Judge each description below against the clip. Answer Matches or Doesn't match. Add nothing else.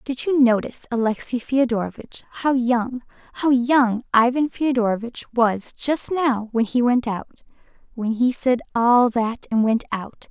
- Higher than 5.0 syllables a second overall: Doesn't match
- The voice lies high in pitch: Matches